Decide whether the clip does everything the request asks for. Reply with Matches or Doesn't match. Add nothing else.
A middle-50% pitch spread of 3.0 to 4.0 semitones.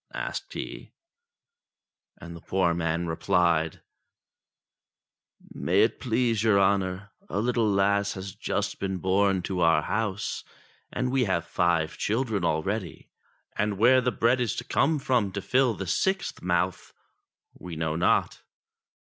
Doesn't match